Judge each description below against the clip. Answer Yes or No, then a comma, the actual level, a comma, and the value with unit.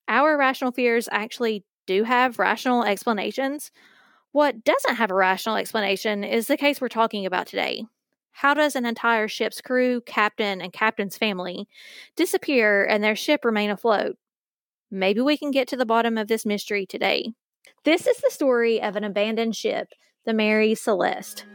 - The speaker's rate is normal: Yes, average, 165 wpm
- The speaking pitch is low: No, high, 225 Hz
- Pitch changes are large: No, average, 3.8 semitones